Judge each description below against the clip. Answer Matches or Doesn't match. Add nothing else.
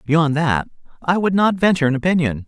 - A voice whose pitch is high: Doesn't match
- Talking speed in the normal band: Matches